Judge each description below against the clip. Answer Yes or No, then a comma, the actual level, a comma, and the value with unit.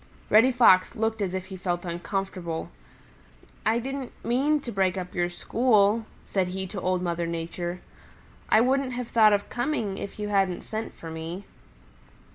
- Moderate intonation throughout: Yes, average, 4.2 semitones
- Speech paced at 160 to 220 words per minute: Yes, average, 165 wpm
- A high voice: Yes, high, 195 Hz